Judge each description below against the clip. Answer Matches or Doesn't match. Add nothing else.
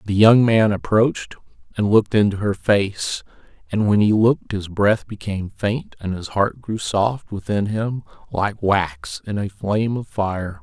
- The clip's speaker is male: Matches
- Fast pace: Doesn't match